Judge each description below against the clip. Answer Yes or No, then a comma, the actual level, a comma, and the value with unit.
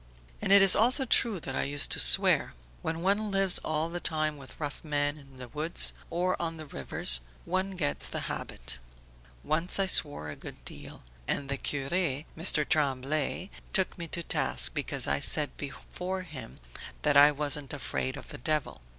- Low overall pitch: No, medium, 150 Hz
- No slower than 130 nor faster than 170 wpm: No, average, 180 wpm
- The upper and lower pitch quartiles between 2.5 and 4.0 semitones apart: No, average, 4.4 semitones